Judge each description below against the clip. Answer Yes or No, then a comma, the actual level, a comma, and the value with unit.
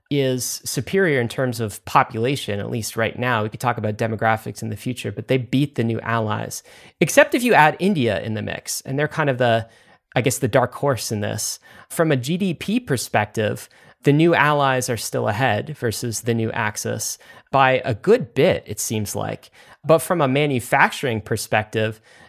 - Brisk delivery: No, average, 190 wpm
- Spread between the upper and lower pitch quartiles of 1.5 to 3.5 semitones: No, average, 4.0 semitones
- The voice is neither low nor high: No, low, 125 Hz